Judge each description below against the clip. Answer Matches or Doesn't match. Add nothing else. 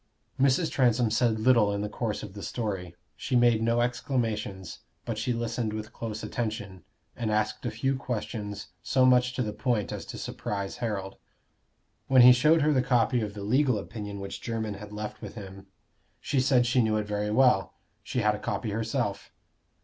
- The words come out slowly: Doesn't match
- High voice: Doesn't match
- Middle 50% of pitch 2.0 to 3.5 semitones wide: Matches